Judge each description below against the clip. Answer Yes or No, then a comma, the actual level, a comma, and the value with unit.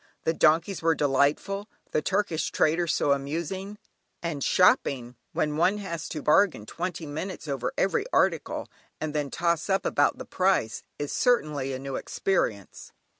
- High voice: No, medium, 160 Hz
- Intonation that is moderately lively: Yes, average, 4.7 semitones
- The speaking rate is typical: Yes, average, 150 wpm